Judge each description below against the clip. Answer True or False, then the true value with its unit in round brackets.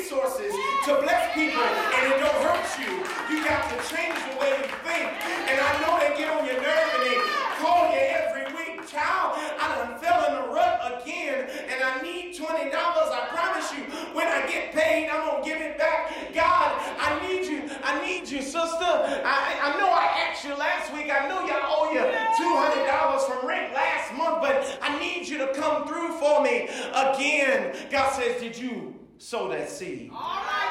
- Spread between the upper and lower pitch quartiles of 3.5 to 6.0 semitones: False (3.0 semitones)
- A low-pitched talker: False (305 Hz)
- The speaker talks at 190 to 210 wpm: True (195 wpm)